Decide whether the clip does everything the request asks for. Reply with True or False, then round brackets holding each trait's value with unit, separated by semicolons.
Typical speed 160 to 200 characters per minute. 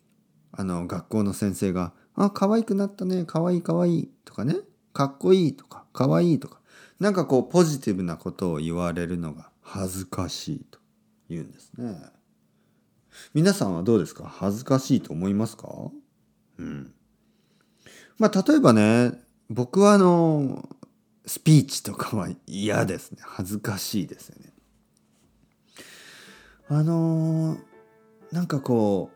False (265 characters per minute)